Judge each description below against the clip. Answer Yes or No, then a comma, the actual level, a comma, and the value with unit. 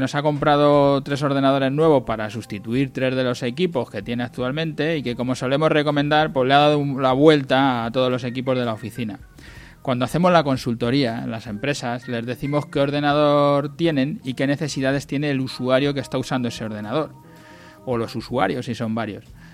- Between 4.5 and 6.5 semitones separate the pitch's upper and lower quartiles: No, average, 3.0 semitones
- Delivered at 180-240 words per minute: Yes, fast, 190 wpm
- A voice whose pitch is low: Yes, low, 130 Hz